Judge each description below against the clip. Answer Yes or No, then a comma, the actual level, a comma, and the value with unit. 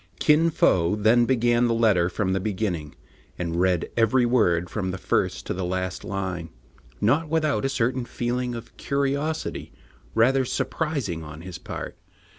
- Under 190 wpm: Yes, average, 155 wpm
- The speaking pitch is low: Yes, low, 115 Hz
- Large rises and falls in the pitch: Yes, wide, 6.0 semitones